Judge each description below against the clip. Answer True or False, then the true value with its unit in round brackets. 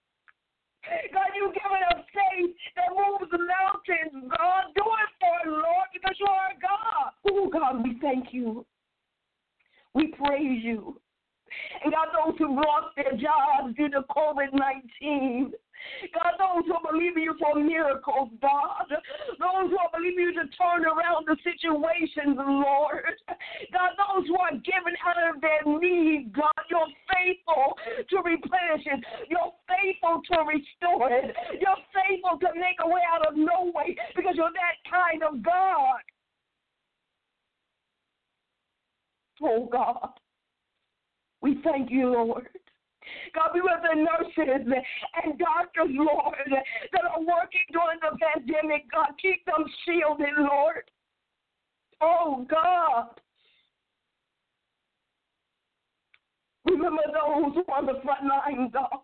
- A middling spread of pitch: True (3.5 semitones)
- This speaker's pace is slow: True (130 wpm)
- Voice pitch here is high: True (330 Hz)